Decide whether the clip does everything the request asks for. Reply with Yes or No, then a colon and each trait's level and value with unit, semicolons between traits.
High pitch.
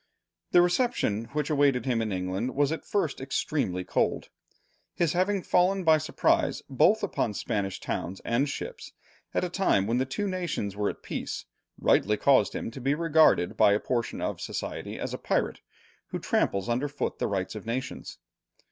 No: low, 135 Hz